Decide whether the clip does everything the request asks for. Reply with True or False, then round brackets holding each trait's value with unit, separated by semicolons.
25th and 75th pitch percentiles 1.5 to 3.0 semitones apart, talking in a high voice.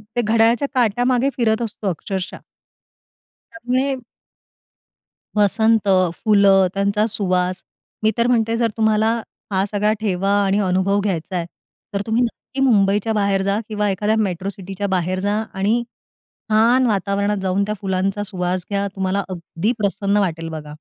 True (2.5 semitones; 200 Hz)